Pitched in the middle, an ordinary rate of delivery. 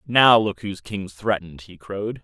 No: low, 100 Hz; average, 190 wpm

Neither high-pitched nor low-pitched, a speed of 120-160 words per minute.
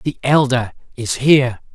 No: low, 130 Hz; average, 140 wpm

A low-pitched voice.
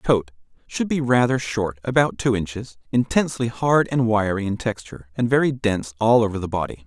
Yes: low, 110 Hz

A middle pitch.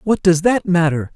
Yes: medium, 175 Hz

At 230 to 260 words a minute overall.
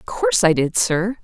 Yes: fast, 245 wpm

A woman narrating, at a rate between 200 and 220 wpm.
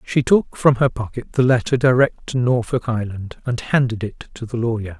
No: male; fast, 205 wpm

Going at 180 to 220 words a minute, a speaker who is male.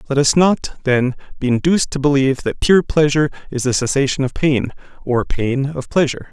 Yes: average, 190 wpm; male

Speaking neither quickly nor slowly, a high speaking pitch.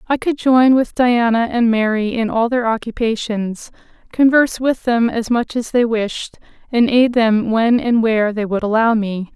Yes: average, 185 wpm; high, 230 Hz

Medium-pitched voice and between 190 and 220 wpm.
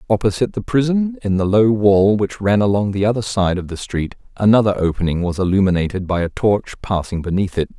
No: low, 100 Hz; average, 200 wpm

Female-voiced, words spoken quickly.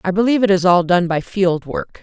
Yes: female; fast, 265 wpm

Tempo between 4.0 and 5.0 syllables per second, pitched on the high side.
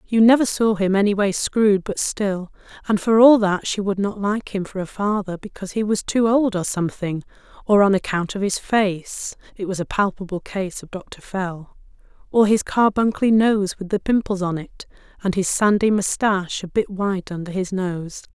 Yes: 4.5 syllables/s; high, 200 Hz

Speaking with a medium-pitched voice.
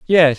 Yes: medium, 160 Hz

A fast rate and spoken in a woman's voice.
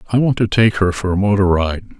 No: fast, 270 wpm; male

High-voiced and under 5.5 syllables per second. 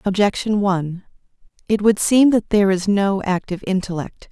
Yes: high, 200 Hz; 5.3 syllables/s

